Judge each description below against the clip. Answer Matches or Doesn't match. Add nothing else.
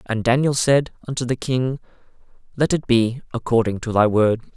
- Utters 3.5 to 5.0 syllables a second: Doesn't match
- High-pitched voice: Doesn't match